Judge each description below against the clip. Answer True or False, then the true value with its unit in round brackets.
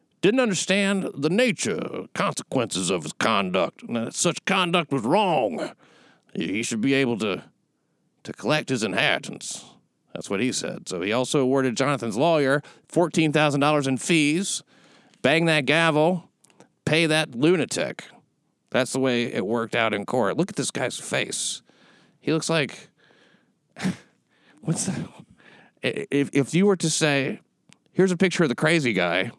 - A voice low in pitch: False (150 Hz)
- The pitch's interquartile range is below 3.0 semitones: False (4.6 semitones)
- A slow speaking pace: False (145 wpm)